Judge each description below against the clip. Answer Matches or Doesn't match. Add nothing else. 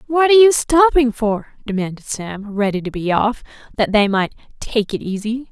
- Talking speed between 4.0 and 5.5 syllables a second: Matches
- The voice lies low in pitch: Doesn't match